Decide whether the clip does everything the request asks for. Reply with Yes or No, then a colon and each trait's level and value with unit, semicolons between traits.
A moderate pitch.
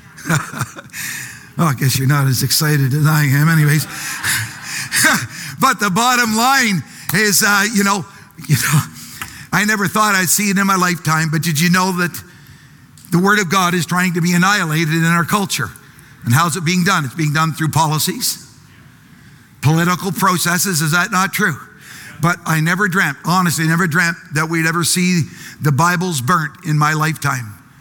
Yes: medium, 165 Hz